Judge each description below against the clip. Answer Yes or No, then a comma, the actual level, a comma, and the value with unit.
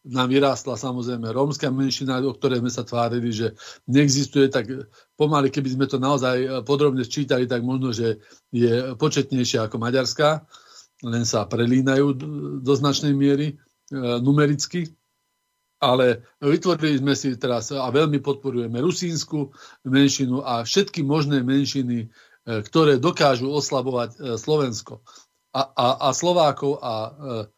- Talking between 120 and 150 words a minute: Yes, average, 135 wpm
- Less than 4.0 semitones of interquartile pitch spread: Yes, narrow, 2.6 semitones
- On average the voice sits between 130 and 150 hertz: Yes, low, 135 Hz